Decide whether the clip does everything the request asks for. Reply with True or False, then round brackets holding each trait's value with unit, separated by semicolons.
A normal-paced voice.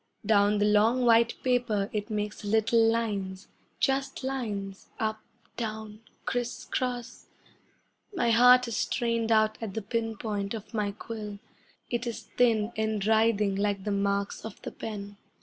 True (150 wpm)